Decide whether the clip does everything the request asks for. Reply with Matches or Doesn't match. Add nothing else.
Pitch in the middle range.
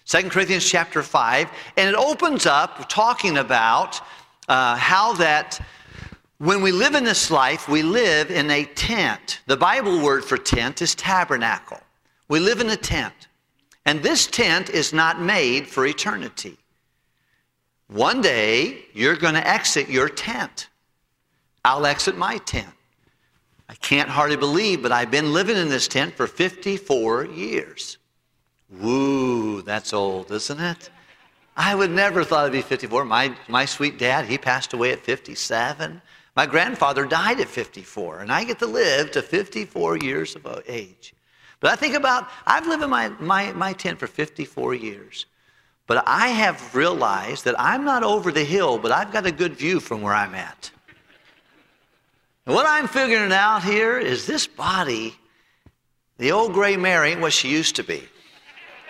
Matches